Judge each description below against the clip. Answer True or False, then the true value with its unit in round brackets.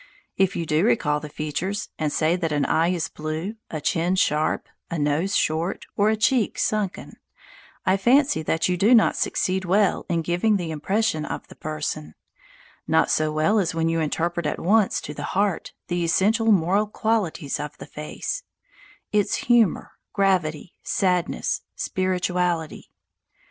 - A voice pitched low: False (175 Hz)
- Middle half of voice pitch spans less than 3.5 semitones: False (4.3 semitones)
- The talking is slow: False (160 wpm)